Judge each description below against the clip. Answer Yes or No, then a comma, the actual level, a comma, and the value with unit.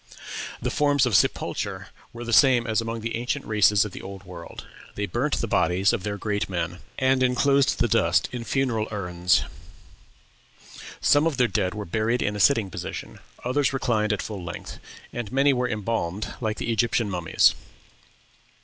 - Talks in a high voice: No, low, 110 Hz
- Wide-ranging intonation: No, average, 4.1 semitones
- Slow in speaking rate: No, average, 175 wpm